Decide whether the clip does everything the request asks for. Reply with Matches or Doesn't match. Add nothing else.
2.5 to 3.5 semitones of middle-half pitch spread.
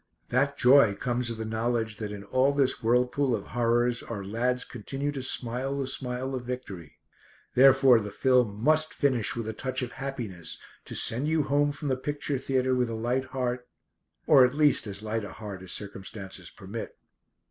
Matches